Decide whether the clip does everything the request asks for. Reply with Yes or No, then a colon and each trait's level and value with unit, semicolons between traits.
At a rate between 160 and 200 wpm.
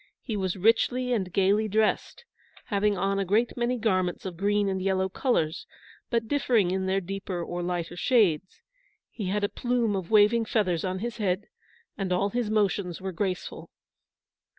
Yes: average, 170 wpm